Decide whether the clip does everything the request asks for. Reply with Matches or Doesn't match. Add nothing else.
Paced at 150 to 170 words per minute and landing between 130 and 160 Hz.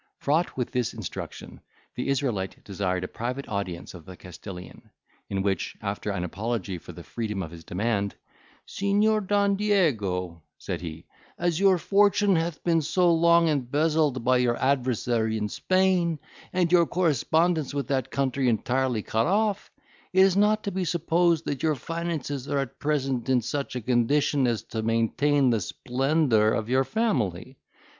Matches